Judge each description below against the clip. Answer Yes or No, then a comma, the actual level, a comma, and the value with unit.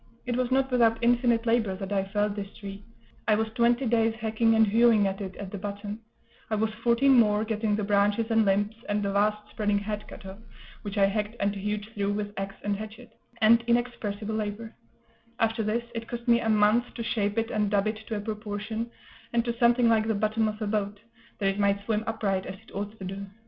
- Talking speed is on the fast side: Yes, fast, 220 wpm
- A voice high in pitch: Yes, high, 215 Hz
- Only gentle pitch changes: Yes, narrow, 2.0 semitones